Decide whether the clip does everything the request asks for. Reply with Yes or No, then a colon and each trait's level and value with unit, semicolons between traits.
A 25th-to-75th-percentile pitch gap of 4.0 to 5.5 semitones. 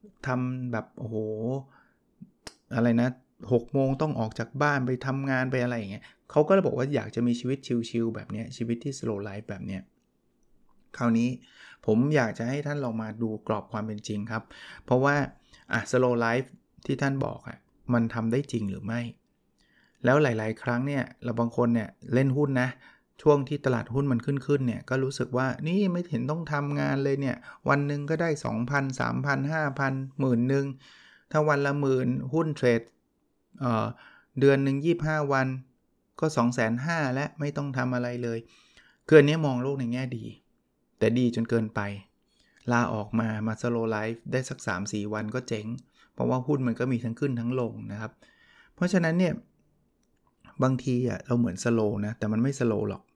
No: average, 3.3 semitones